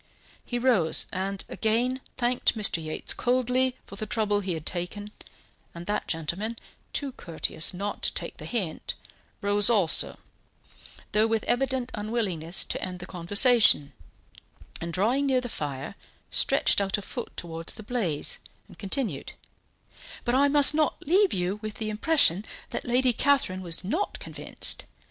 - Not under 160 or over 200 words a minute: No, average, 150 wpm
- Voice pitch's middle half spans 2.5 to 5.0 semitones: No, wide, 5.5 semitones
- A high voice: Yes, high, 210 Hz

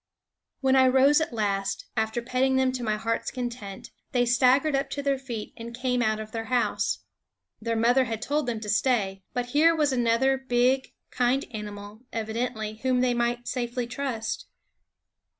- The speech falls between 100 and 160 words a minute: No, average, 170 wpm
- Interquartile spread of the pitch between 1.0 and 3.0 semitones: Yes, average, 2.7 semitones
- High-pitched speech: Yes, high, 245 Hz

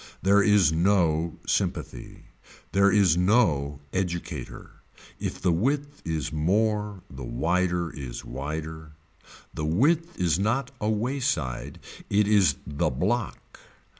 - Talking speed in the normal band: No, slow, 115 wpm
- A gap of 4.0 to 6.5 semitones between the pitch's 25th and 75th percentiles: Yes, average, 5.2 semitones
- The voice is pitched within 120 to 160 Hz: No, very low, 90 Hz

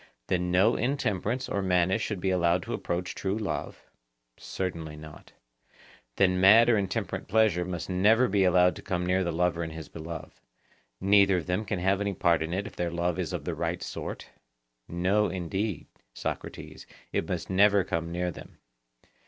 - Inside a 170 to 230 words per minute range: Yes, average, 175 wpm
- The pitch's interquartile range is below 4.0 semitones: Yes, narrow, 2.5 semitones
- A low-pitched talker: Yes, very low, 90 Hz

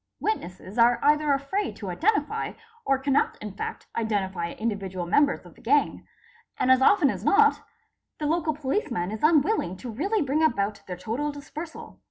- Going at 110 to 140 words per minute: No, average, 165 wpm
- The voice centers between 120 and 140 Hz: No, very high, 265 Hz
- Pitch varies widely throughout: Yes, wide, 7.1 semitones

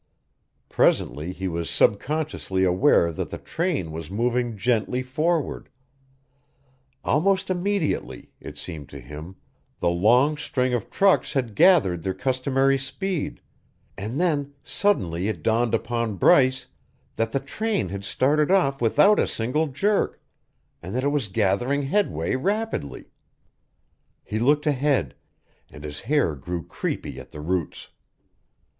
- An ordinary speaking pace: No, slow, 130 wpm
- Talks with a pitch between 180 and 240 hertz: No, low, 125 Hz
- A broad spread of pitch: Yes, wide, 8.0 semitones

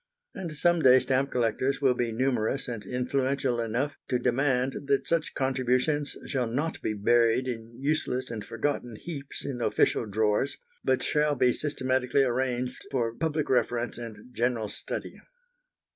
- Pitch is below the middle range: Yes, low, 125 Hz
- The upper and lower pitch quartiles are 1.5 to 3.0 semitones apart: Yes, average, 2.7 semitones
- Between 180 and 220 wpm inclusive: No, average, 145 wpm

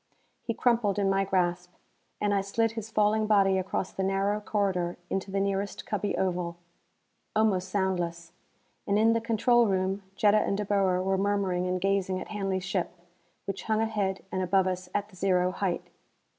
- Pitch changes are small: Yes, narrow, 1.9 semitones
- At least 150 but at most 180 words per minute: Yes, average, 175 wpm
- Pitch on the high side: Yes, high, 195 Hz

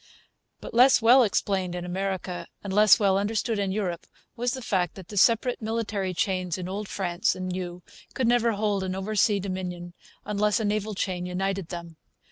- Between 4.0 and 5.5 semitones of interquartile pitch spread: No, average, 2.8 semitones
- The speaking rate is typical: Yes, average, 180 wpm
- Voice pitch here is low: No, high, 195 Hz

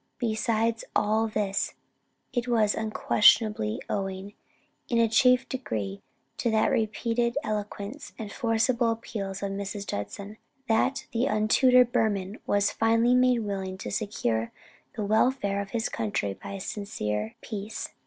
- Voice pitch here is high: Yes, high, 215 Hz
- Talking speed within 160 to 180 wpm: No, slow, 135 wpm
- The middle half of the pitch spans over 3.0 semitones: No, average, 2.7 semitones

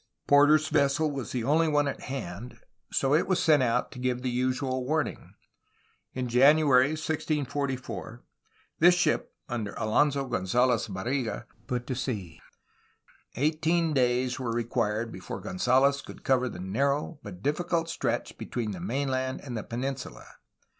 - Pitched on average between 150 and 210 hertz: No, low, 130 Hz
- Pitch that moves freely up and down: No, average, 3.2 semitones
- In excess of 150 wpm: No, average, 140 wpm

